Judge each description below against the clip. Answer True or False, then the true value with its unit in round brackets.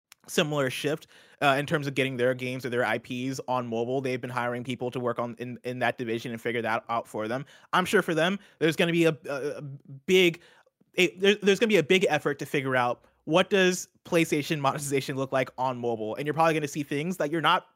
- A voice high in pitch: False (140 Hz)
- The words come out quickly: True (245 wpm)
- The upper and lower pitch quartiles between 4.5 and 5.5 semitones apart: True (4.9 semitones)